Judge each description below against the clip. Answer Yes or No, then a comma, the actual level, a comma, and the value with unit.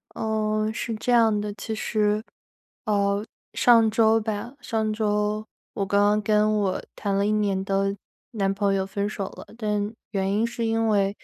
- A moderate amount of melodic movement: No, narrow, 1.5 semitones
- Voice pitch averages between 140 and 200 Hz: No, high, 210 Hz